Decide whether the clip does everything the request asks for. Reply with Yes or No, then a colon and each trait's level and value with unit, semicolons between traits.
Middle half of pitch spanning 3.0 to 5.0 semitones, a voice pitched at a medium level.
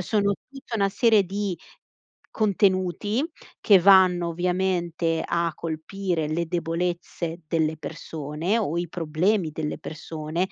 Yes: average, 3.3 semitones; medium, 175 Hz